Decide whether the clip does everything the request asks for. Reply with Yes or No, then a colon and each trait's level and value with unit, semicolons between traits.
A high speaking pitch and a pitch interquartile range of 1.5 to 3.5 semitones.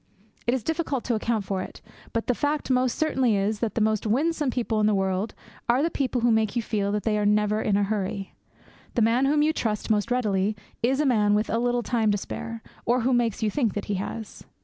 Yes: high, 225 Hz; average, 3.2 semitones